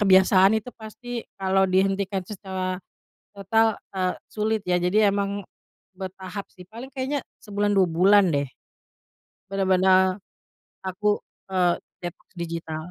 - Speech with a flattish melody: Yes, narrow, 1.9 semitones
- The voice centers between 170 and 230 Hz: Yes, high, 190 Hz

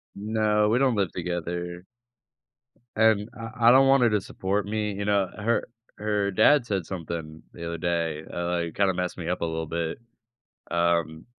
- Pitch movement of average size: Yes, average, 3.9 semitones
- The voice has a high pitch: No, very low, 95 Hz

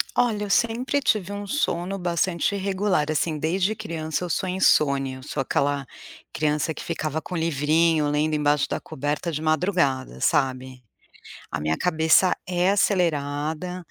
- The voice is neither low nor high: Yes, medium, 160 Hz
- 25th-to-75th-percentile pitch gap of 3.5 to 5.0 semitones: Yes, average, 4.0 semitones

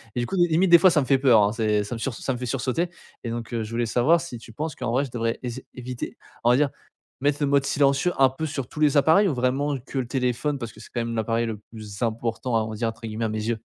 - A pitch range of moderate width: Yes, average, 3.6 semitones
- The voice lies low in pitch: Yes, low, 125 Hz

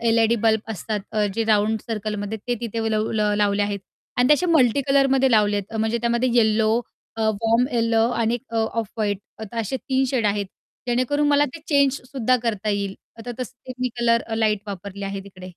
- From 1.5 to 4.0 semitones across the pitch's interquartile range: Yes, average, 2.8 semitones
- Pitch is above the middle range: Yes, high, 225 Hz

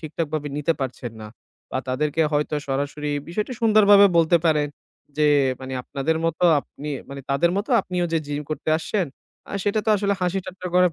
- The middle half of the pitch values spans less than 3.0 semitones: No, average, 3.8 semitones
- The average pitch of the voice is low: No, medium, 160 Hz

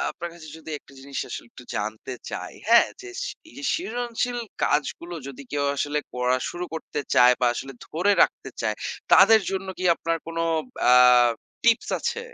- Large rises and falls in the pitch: Yes, wide, 8.4 semitones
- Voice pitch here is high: No, medium, 165 Hz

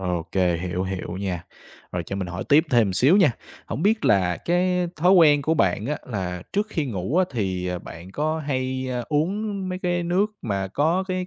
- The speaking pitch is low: Yes, low, 130 Hz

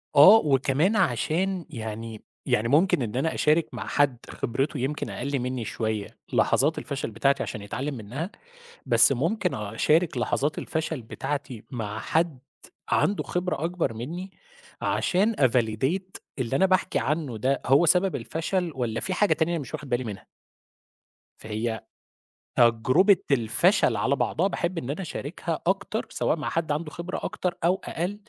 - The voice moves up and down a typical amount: No, wide, 6.2 semitones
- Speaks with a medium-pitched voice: Yes, medium, 145 Hz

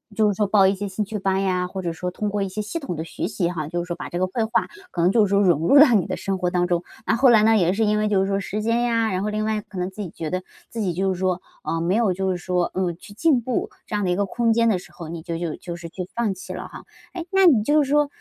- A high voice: Yes, high, 195 Hz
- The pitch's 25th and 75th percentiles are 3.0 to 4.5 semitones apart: Yes, average, 3.4 semitones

